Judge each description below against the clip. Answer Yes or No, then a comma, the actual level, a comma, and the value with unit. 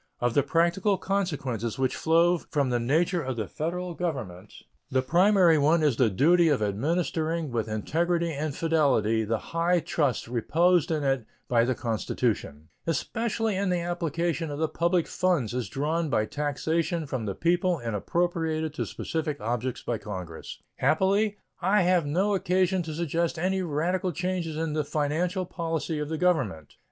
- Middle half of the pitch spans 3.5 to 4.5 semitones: No, average, 5.0 semitones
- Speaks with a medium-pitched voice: Yes, medium, 160 Hz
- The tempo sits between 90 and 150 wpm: No, average, 165 wpm